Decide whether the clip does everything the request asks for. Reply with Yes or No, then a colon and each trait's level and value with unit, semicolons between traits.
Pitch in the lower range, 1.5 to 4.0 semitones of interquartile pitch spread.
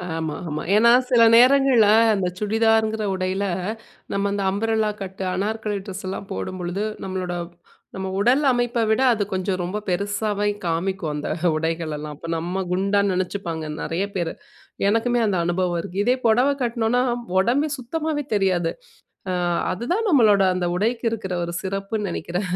No: high, 200 Hz; average, 3.7 semitones